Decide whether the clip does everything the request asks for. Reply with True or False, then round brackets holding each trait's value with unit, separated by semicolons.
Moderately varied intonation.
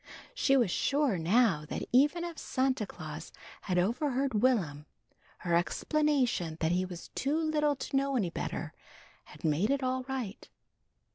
False (7.5 semitones)